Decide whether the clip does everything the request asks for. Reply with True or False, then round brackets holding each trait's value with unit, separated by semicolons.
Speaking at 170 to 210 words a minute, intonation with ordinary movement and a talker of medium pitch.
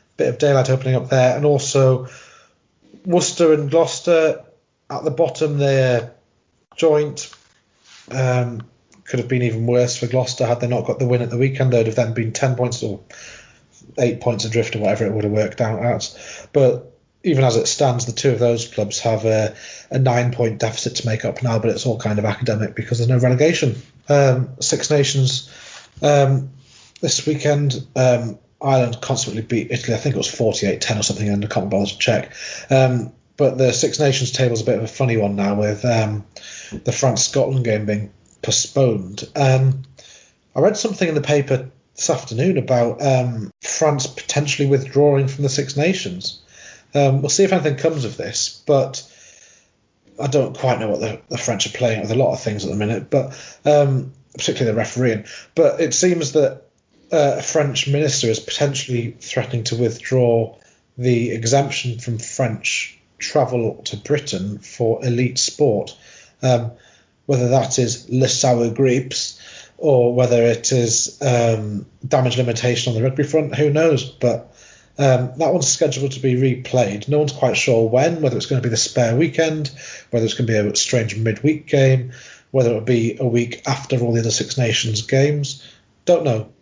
False (185 wpm; 3.3 semitones; 125 Hz)